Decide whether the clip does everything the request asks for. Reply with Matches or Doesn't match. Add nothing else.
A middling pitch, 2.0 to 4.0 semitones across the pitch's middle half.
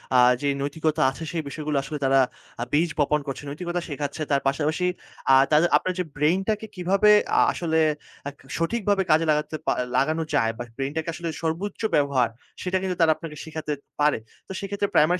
Matches